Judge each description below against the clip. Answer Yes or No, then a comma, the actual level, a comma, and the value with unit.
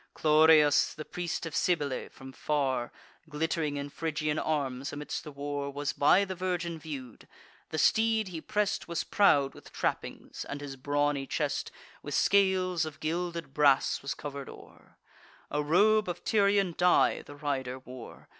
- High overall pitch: No, medium, 150 Hz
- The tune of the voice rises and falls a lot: No, average, 3.7 semitones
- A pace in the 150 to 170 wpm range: Yes, average, 155 wpm